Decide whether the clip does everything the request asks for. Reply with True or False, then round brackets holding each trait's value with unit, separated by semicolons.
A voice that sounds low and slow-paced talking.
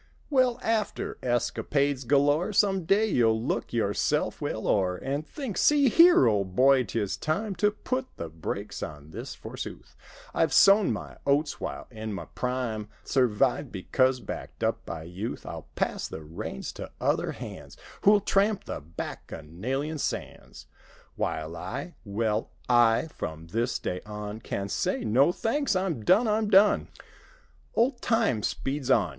False (130 Hz; 145 wpm)